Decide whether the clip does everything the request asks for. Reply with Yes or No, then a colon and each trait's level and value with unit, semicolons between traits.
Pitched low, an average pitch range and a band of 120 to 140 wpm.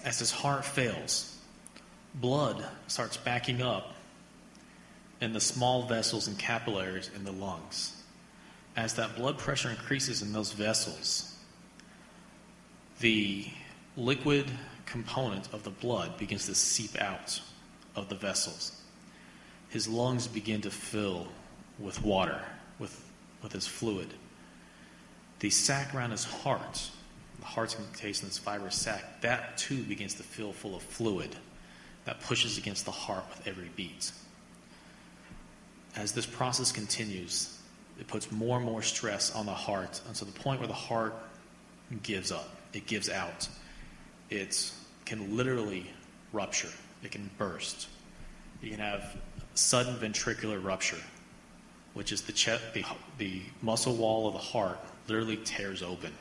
Yes: low, 110 Hz; average, 3.0 semitones; slow, 135 wpm